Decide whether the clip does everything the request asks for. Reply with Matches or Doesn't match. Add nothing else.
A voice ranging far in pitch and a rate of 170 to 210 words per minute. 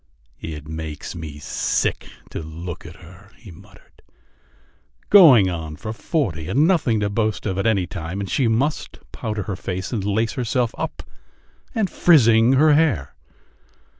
Doesn't match